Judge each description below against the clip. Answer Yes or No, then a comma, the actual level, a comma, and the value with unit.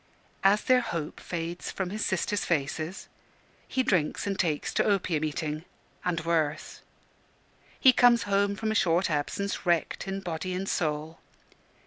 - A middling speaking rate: Yes, average, 145 wpm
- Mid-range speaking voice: Yes, medium, 180 Hz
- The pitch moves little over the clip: No, average, 4.0 semitones